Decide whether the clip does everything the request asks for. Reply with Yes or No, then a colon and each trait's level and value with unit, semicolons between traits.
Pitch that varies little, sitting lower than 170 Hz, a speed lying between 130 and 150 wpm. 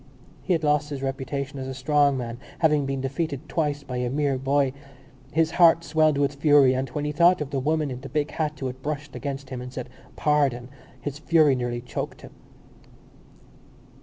No: narrow, 2.3 semitones; medium, 140 Hz; average, 195 wpm